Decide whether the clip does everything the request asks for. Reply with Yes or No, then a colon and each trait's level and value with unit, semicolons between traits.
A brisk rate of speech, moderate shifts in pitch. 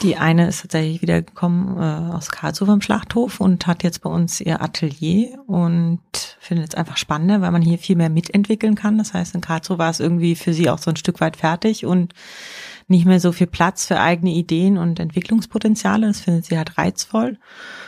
Yes: fast, 200 wpm; average, 3.2 semitones